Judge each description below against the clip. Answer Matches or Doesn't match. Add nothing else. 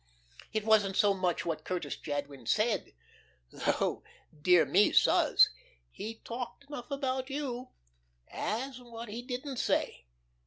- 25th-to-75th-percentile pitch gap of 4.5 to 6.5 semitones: Matches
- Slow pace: Matches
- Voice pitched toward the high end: Matches